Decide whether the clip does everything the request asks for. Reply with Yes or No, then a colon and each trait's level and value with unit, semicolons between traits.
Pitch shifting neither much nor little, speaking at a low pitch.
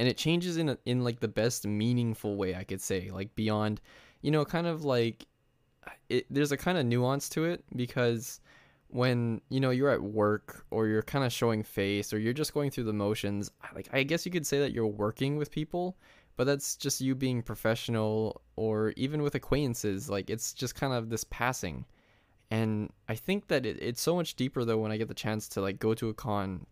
Yes: average, 4.3 semitones; low, 120 Hz